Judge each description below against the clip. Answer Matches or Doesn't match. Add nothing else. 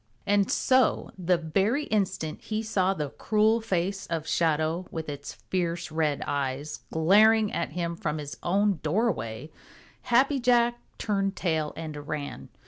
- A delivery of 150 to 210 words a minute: Doesn't match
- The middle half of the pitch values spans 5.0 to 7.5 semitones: Matches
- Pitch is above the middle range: Doesn't match